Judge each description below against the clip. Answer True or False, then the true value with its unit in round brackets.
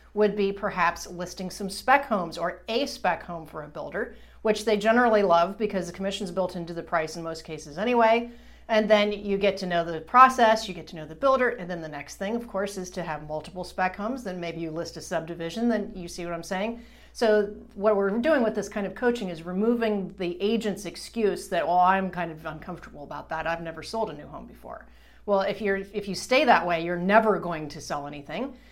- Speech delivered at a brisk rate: True (230 wpm)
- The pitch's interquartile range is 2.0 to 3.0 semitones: False (4.1 semitones)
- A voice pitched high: True (195 Hz)